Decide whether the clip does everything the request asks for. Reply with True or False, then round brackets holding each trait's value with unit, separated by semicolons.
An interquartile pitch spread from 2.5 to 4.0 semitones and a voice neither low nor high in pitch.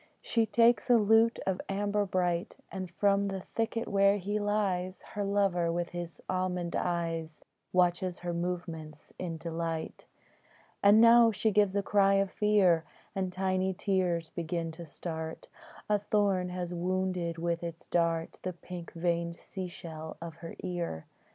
True (2.9 semitones; 180 Hz)